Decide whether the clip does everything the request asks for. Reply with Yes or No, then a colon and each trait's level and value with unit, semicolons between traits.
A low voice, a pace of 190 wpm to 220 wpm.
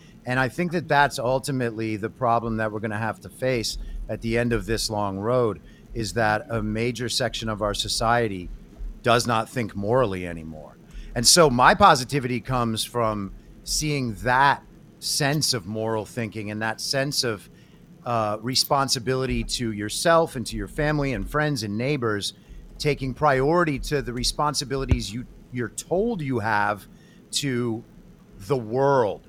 No: low, 120 Hz; average, 155 wpm